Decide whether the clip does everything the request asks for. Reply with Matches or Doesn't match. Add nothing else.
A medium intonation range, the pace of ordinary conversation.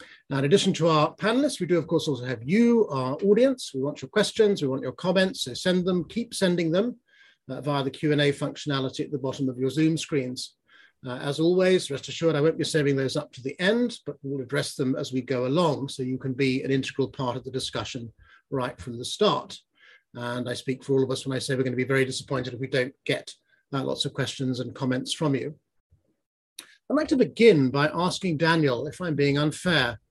Doesn't match